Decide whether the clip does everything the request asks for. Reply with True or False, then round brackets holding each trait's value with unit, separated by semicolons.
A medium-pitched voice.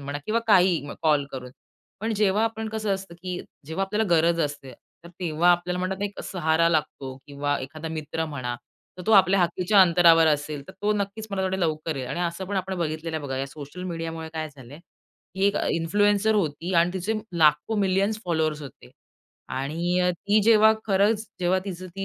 True (175 Hz)